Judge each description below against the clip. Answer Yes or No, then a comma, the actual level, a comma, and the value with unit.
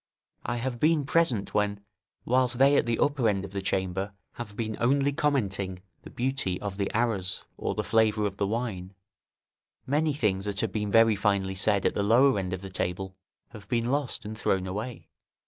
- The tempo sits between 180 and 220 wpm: Yes, average, 195 wpm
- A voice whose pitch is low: Yes, low, 105 Hz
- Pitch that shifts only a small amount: No, average, 4.2 semitones